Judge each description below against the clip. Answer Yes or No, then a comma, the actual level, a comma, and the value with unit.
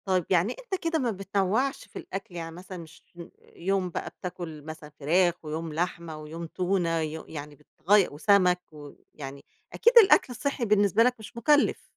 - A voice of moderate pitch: Yes, medium, 180 Hz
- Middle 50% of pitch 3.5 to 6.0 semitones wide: Yes, average, 4.3 semitones